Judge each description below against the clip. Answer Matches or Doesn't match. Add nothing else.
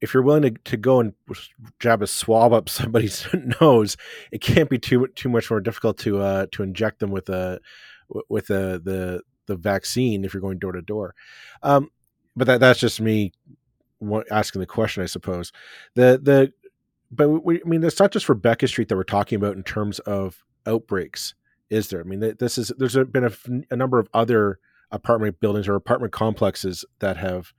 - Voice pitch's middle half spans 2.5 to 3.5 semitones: Doesn't match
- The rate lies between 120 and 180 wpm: Doesn't match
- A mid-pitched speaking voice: Doesn't match